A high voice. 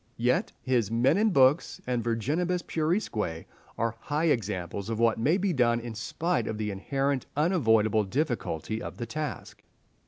No: low, 120 Hz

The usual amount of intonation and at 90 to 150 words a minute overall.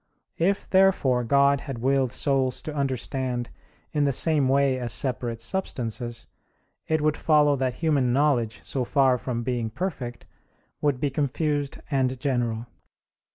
Yes: average, 3.0 semitones; average, 140 wpm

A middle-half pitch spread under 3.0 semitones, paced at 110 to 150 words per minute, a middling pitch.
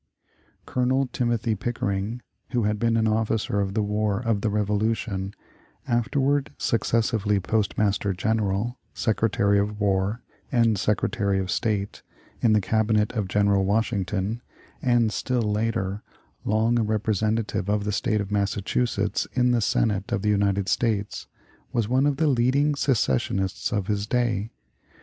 No: narrow, 2.5 semitones; average, 140 wpm; low, 105 Hz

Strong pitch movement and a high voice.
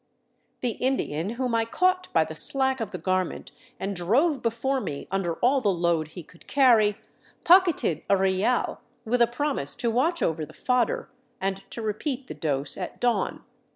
Yes: wide, 6.6 semitones; high, 225 Hz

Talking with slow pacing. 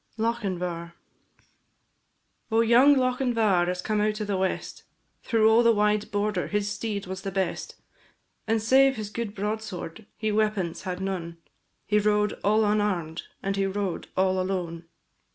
No: average, 150 wpm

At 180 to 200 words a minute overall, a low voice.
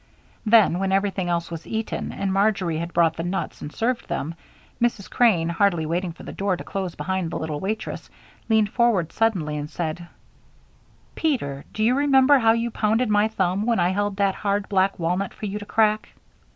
No: average, 190 wpm; high, 195 Hz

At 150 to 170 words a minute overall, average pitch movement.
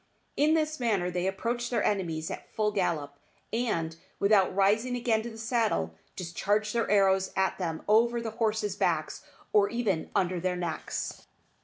Yes: average, 160 wpm; average, 4.2 semitones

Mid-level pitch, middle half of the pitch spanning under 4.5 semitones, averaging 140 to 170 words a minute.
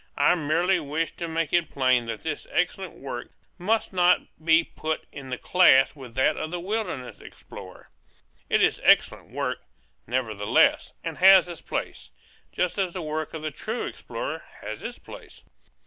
No: medium, 160 Hz; average, 5.1 semitones; average, 165 wpm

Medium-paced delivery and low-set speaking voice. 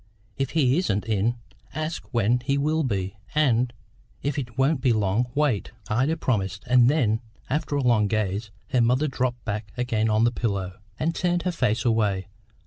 Yes: average, 175 wpm; low, 120 Hz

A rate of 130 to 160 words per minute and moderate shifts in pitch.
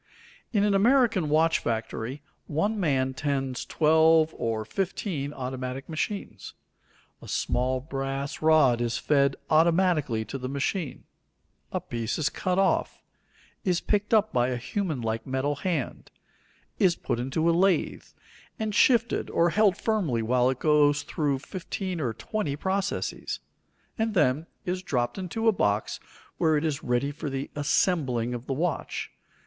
No: average, 145 wpm; wide, 6.0 semitones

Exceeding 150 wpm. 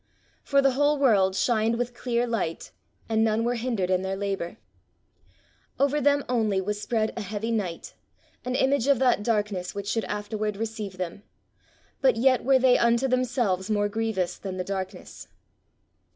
Yes: average, 165 wpm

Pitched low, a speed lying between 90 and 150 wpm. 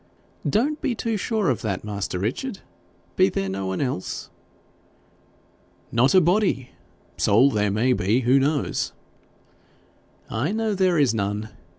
Yes: low, 130 Hz; slow, 135 wpm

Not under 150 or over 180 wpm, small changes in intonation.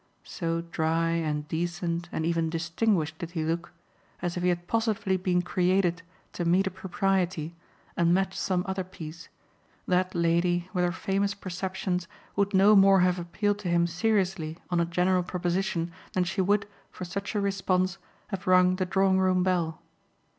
Yes: average, 170 wpm; narrow, 2.0 semitones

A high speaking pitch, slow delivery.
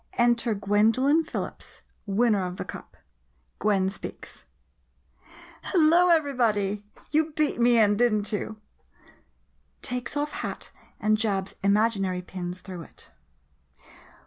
Yes: high, 215 Hz; slow, 120 wpm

